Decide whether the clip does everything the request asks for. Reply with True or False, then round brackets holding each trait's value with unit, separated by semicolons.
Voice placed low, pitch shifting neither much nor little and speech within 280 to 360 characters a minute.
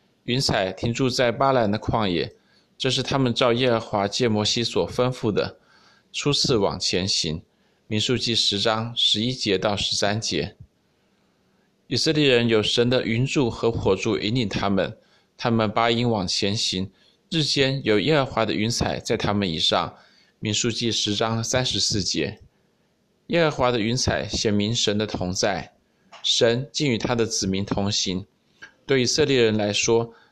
False (115 Hz; 3.3 semitones; 230 characters per minute)